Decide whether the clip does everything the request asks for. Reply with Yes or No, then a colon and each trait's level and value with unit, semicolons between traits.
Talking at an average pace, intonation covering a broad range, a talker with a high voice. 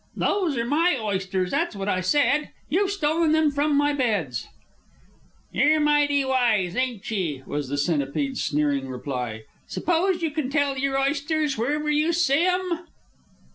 Yes: average, 150 wpm; wide, 8.3 semitones; very high, 275 Hz